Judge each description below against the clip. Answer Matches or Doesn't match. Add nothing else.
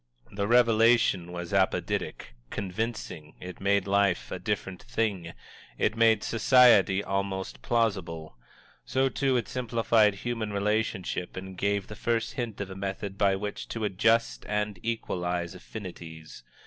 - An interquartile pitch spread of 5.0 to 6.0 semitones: Doesn't match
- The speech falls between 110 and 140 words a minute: Matches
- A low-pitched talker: Matches